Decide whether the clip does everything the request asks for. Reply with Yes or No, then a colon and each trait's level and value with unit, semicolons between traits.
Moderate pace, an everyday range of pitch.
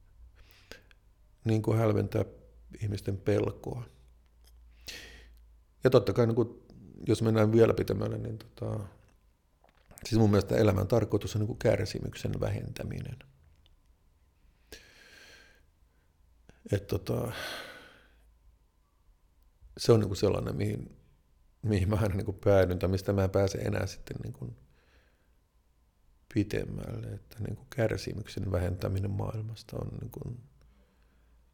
No: average, 105 wpm; wide, 6.1 semitones